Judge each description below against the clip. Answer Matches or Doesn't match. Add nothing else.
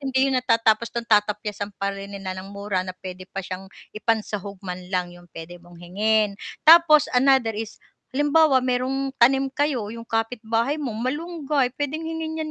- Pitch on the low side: Doesn't match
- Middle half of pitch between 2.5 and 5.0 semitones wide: Doesn't match